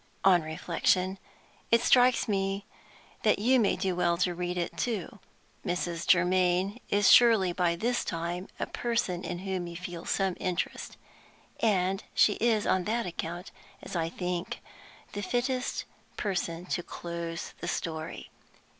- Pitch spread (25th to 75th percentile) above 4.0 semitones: No, average, 2.9 semitones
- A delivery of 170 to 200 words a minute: No, average, 145 wpm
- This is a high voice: No, medium, 180 Hz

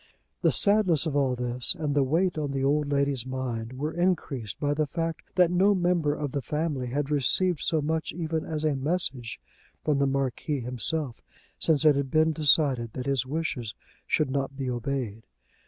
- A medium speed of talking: Yes, average, 185 wpm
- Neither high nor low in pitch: Yes, medium, 145 Hz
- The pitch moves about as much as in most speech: Yes, average, 3.4 semitones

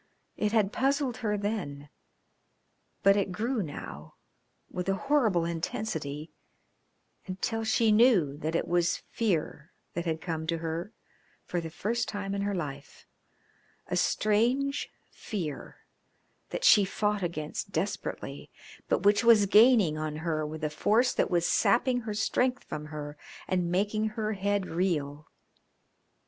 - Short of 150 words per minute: Yes, average, 140 wpm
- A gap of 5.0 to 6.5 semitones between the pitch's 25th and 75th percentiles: Yes, average, 5.3 semitones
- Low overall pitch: No, high, 195 Hz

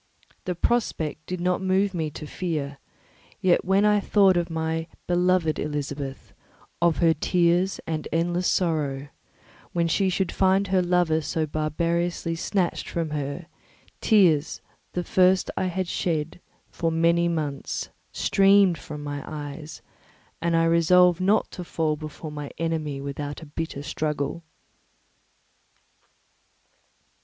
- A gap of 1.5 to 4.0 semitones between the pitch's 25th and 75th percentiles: Yes, average, 3.0 semitones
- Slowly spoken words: Yes, slow, 130 wpm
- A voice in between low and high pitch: Yes, medium, 165 Hz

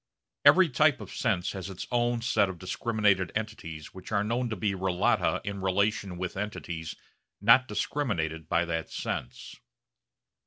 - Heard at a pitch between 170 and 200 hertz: No, low, 100 Hz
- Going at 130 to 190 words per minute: Yes, average, 150 wpm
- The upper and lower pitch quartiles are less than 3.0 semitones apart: No, average, 4.1 semitones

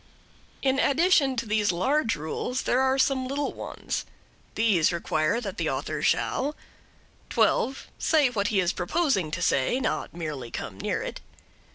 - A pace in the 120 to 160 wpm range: Yes, average, 155 wpm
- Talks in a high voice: Yes, high, 235 Hz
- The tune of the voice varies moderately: No, wide, 7.3 semitones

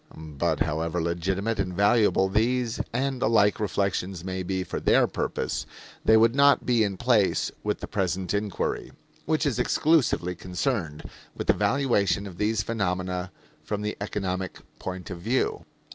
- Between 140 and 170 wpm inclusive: Yes, average, 155 wpm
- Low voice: Yes, low, 100 Hz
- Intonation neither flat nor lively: Yes, average, 3.9 semitones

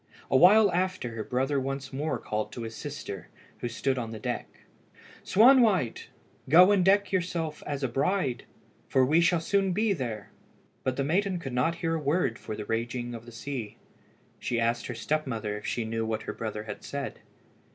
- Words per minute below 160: No, average, 195 wpm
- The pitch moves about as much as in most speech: No, wide, 6.9 semitones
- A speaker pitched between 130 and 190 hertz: Yes, low, 135 Hz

